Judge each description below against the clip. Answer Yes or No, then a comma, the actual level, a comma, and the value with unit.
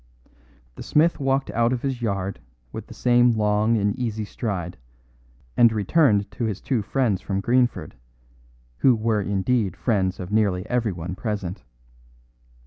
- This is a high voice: No, low, 110 Hz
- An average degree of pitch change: Yes, average, 3.7 semitones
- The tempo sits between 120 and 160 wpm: Yes, average, 140 wpm